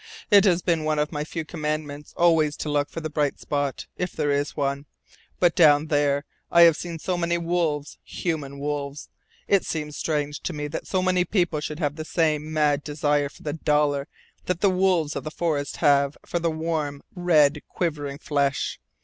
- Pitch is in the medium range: Yes, medium, 150 Hz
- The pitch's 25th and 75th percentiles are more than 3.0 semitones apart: No, narrow, 2.6 semitones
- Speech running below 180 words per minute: No, average, 190 wpm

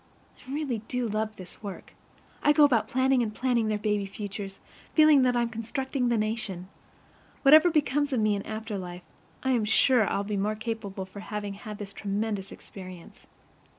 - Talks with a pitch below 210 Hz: No, high, 220 Hz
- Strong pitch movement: No, average, 3.8 semitones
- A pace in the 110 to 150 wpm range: No, average, 185 wpm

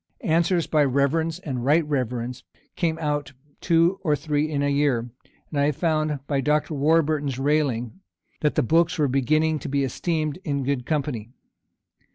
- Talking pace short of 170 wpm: Yes, average, 160 wpm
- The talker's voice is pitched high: No, medium, 150 Hz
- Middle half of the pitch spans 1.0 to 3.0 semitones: Yes, narrow, 2.5 semitones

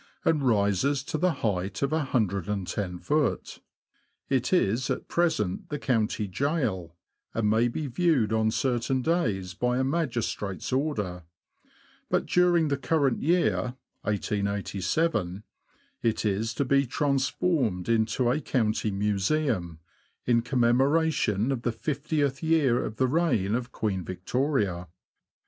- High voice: No, low, 120 Hz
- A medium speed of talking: No, slow, 120 wpm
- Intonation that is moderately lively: No, wide, 5.8 semitones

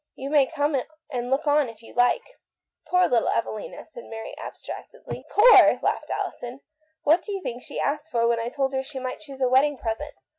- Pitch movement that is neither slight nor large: Yes, average, 3.6 semitones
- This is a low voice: No, very high, 270 Hz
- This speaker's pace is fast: Yes, fast, 235 wpm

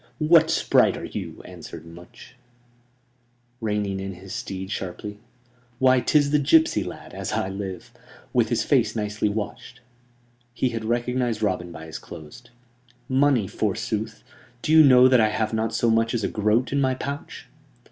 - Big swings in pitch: No, average, 4.8 semitones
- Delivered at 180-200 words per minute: No, average, 160 wpm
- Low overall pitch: Yes, low, 110 Hz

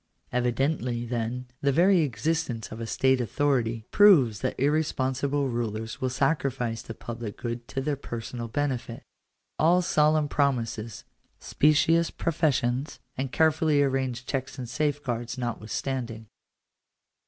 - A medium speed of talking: No, slow, 120 wpm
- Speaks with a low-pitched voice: Yes, low, 130 Hz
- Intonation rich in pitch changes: No, average, 3.7 semitones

